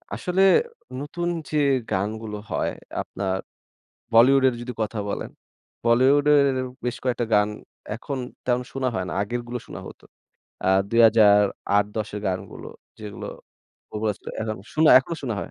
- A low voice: Yes, low, 115 Hz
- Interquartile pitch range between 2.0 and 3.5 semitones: No, average, 4.0 semitones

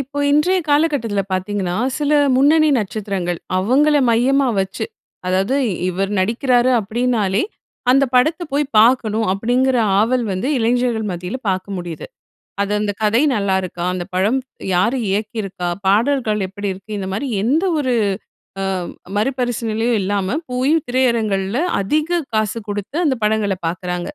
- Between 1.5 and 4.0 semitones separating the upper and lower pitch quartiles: No, average, 4.9 semitones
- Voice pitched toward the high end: Yes, high, 220 Hz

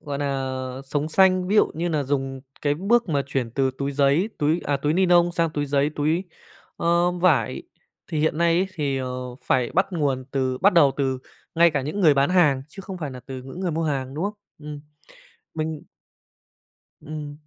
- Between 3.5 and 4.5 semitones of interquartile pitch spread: Yes, average, 3.8 semitones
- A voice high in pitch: No, medium, 150 Hz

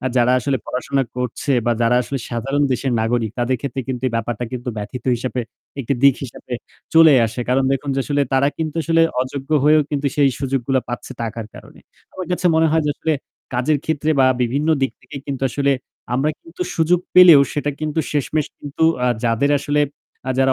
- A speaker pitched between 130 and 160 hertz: Yes, low, 135 Hz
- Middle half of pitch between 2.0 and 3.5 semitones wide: Yes, average, 3.1 semitones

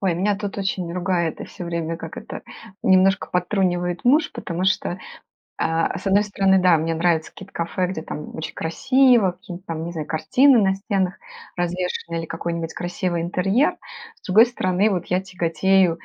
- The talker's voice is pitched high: No, medium, 180 Hz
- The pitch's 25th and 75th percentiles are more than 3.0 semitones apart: No, narrow, 2.4 semitones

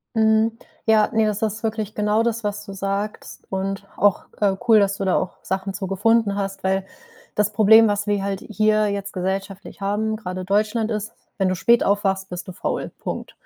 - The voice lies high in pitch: Yes, high, 205 Hz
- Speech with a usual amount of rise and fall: No, narrow, 1.8 semitones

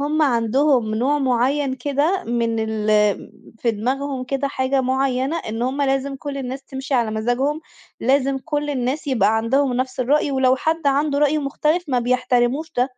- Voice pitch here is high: Yes, very high, 265 Hz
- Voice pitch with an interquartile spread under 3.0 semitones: Yes, narrow, 2.6 semitones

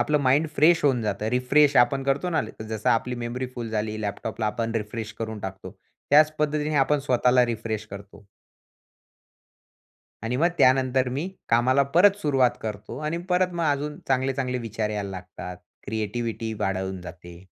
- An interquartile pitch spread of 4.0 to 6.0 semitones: Yes, average, 4.4 semitones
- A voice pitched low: Yes, low, 120 Hz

